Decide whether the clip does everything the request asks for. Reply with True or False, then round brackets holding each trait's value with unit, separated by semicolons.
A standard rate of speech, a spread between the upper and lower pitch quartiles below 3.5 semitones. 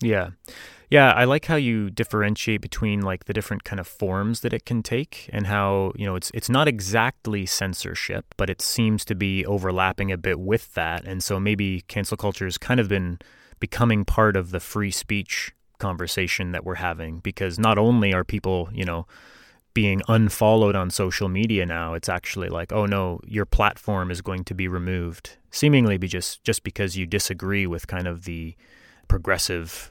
True (185 wpm; 2.9 semitones)